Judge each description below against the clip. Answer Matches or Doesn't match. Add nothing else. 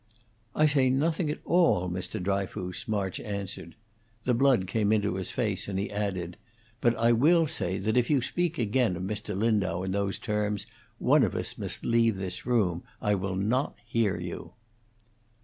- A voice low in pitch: Matches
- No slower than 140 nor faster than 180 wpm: Matches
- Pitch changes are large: Doesn't match